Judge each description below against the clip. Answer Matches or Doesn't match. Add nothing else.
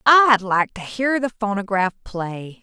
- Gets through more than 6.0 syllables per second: Doesn't match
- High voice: Matches